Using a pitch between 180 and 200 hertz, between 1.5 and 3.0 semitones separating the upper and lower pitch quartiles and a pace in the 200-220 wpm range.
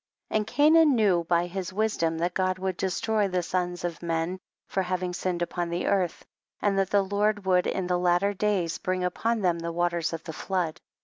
Yes: medium, 185 Hz; narrow, 2.4 semitones; fast, 205 wpm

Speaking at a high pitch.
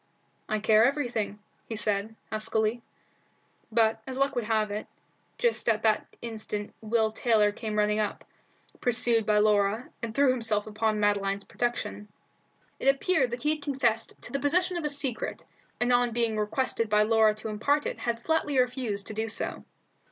Yes: high, 225 Hz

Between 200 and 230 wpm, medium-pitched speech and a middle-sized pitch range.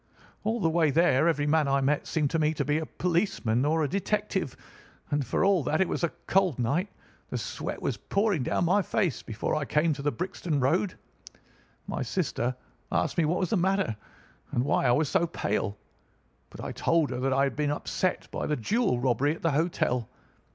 Yes: fast, 205 wpm; medium, 155 Hz; average, 4.7 semitones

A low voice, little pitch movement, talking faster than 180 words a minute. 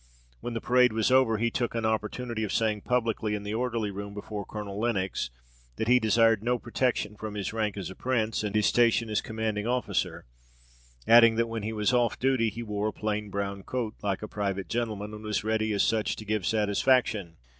Yes: low, 110 Hz; narrow, 2.0 semitones; fast, 205 wpm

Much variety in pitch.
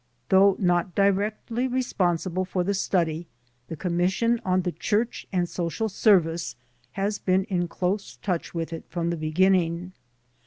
No: narrow, 2.6 semitones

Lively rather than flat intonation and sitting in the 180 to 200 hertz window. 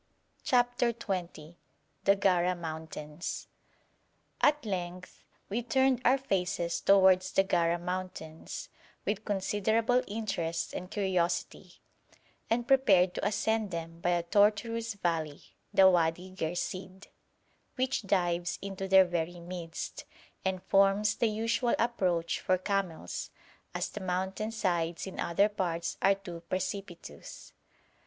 No: average, 3.3 semitones; high, 190 Hz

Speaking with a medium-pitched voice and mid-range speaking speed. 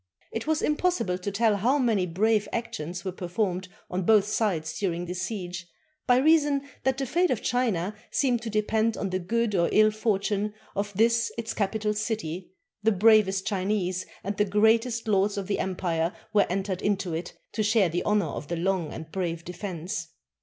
No: high, 205 Hz; average, 180 wpm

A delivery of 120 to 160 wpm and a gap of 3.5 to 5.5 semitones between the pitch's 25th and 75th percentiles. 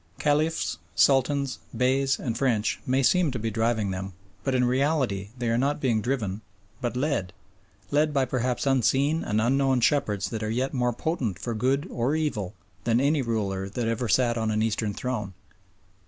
No: average, 175 wpm; average, 3.9 semitones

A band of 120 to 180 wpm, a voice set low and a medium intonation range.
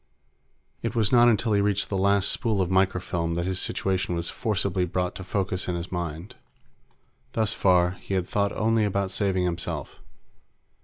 No: average, 170 wpm; very low, 95 Hz; narrow, 2.3 semitones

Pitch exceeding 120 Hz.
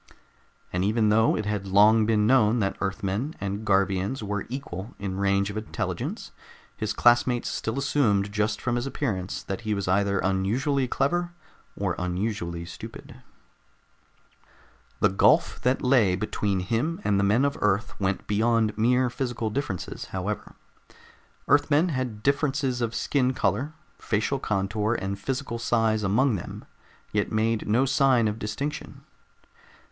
No: low, 110 Hz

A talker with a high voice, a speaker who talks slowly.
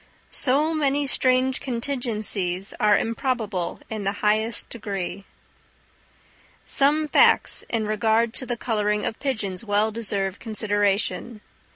Yes: high, 220 Hz; slow, 110 wpm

